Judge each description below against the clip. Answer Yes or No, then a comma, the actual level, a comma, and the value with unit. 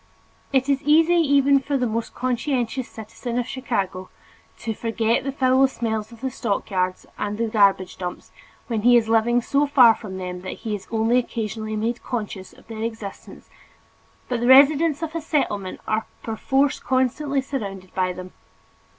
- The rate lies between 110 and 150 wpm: No, average, 170 wpm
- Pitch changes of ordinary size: Yes, average, 3.9 semitones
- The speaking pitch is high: Yes, high, 235 Hz